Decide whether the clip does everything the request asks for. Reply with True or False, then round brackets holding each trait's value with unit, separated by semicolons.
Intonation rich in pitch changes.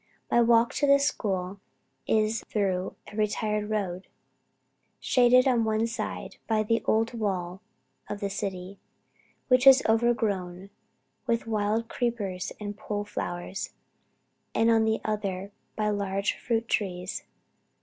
False (2.6 semitones)